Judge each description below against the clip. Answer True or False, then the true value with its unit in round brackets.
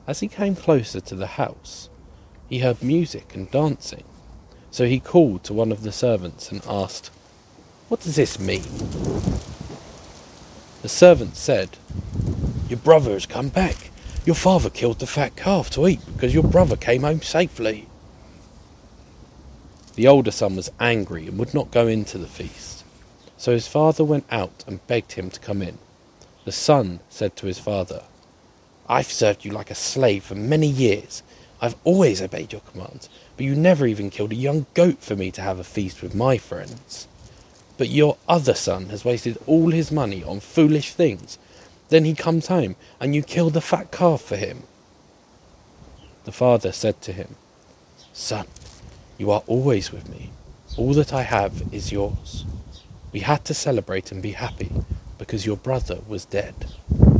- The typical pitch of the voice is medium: False (115 Hz)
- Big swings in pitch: True (7.2 semitones)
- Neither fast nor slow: True (170 wpm)